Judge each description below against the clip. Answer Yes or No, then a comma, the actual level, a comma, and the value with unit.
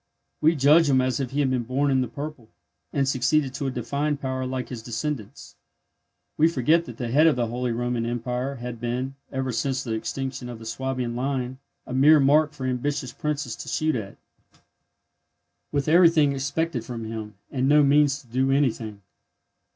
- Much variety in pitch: No, average, 2.8 semitones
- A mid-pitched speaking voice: No, low, 130 Hz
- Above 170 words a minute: Yes, average, 185 wpm